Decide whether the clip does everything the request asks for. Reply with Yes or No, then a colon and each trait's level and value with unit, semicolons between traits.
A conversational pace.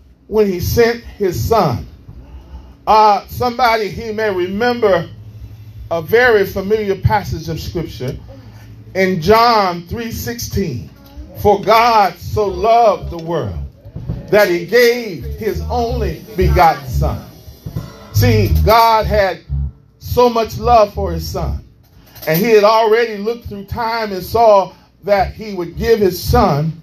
No: slow, 125 wpm